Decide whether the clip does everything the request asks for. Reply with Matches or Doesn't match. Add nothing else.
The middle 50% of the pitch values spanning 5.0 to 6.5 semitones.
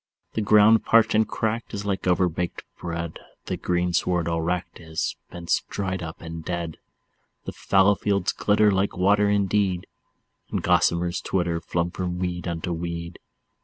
Doesn't match